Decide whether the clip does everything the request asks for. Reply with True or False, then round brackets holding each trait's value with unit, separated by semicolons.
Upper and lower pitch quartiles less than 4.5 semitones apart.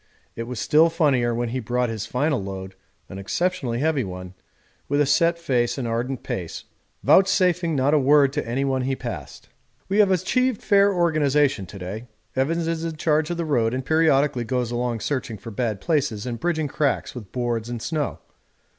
False (5.3 semitones)